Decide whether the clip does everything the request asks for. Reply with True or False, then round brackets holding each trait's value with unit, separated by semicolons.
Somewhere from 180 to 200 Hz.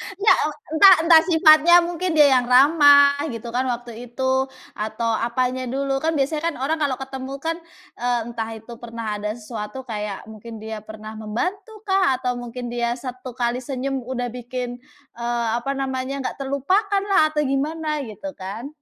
False (255 Hz)